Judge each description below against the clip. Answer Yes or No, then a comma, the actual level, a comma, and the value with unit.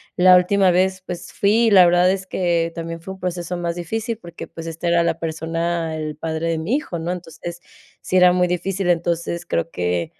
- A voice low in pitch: No, medium, 175 Hz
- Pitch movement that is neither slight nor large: No, narrow, 1.7 semitones